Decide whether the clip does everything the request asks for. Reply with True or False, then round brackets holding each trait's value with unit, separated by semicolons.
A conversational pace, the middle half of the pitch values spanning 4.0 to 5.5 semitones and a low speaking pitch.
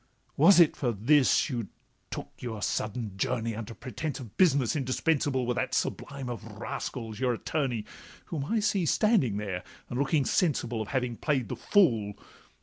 True (160 wpm; 4.6 semitones; 125 Hz)